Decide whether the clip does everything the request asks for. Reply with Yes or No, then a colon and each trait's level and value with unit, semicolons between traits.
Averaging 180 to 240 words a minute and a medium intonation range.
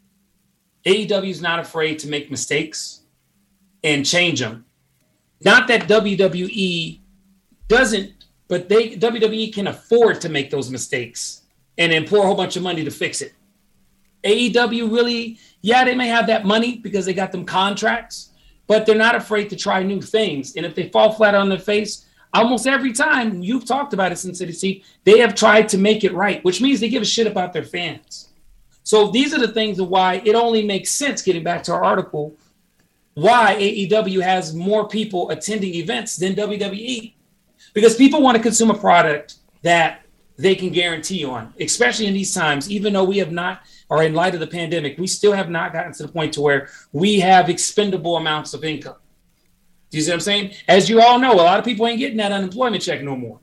Yes: average, 200 wpm; average, 4.3 semitones